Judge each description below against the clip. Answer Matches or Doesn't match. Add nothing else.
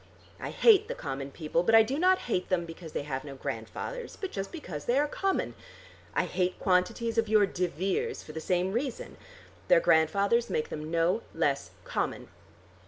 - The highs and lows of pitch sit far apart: Matches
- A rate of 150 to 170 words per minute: Doesn't match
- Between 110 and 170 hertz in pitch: Doesn't match